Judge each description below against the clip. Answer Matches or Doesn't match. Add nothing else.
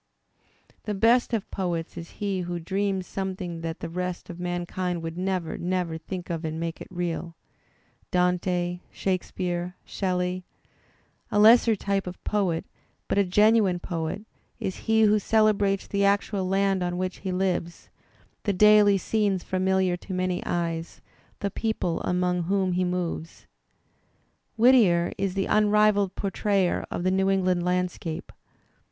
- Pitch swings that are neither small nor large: Doesn't match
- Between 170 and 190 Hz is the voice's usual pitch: Matches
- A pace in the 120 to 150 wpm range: Matches